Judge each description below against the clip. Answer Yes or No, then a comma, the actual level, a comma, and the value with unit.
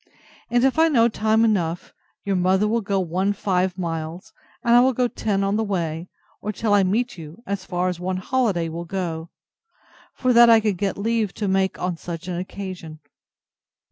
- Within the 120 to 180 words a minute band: No, average, 195 wpm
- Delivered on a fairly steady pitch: No, average, 3.8 semitones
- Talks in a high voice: Yes, high, 195 Hz